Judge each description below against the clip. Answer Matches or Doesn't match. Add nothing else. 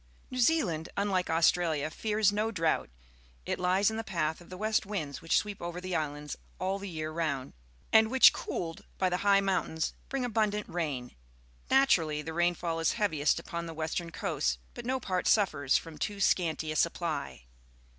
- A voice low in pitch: Doesn't match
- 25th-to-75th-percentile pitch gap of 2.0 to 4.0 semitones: Doesn't match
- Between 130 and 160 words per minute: Doesn't match